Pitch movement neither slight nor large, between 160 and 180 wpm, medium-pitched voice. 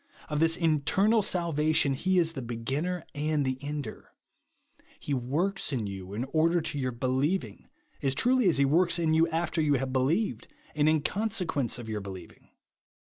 Yes: average, 4.6 semitones; average, 170 wpm; medium, 150 Hz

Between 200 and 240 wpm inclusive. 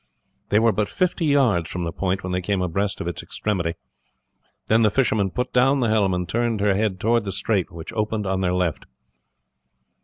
Yes: fast, 205 wpm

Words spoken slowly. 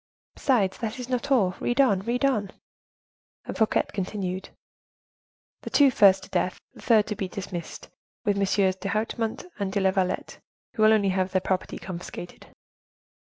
No: average, 155 wpm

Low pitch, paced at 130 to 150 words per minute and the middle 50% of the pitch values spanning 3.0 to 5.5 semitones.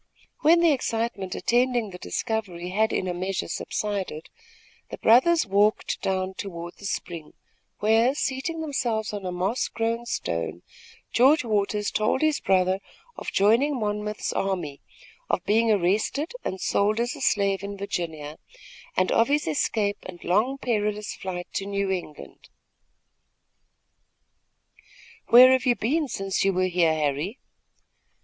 No: high, 205 Hz; average, 140 wpm; average, 4.3 semitones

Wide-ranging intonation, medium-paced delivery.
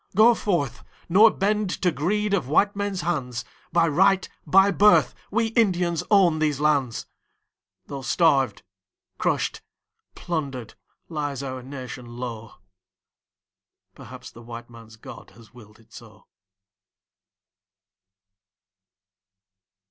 No: wide, 7.5 semitones; slow, 110 wpm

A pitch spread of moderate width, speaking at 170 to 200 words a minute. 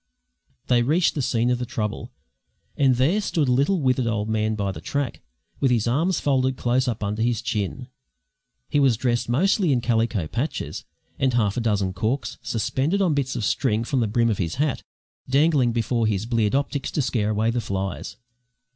Yes: average, 3.7 semitones; average, 190 wpm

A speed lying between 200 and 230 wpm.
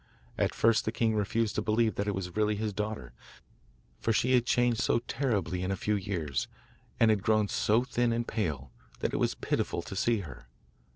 Yes: fast, 205 wpm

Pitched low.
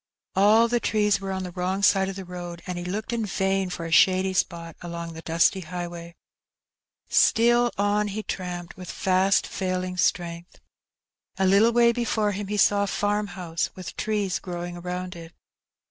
No: medium, 185 Hz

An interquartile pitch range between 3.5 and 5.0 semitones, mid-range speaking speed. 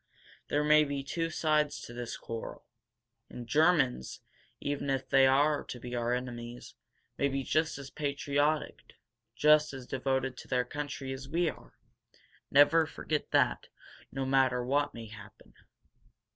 No: average, 3.1 semitones; average, 145 wpm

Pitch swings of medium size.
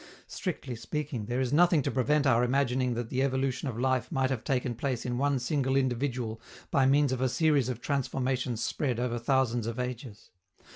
No: narrow, 2.0 semitones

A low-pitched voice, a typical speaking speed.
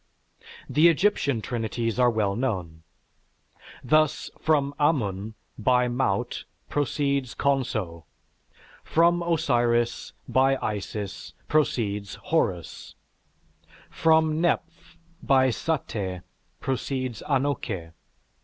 No: low, 125 Hz; slow, 80 wpm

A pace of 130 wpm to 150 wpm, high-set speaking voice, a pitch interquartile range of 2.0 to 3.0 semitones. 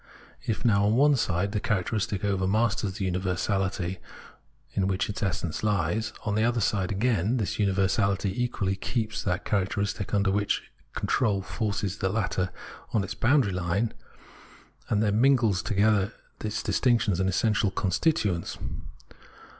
No: average, 140 wpm; low, 100 Hz; average, 2.7 semitones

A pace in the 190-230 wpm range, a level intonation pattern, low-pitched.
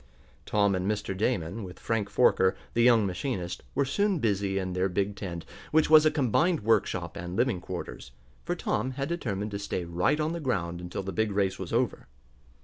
No: average, 195 wpm; wide, 5.5 semitones; low, 100 Hz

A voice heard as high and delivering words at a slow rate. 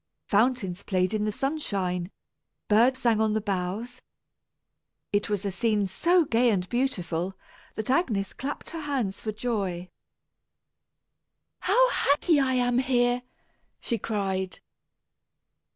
Yes: high, 220 Hz; slow, 120 wpm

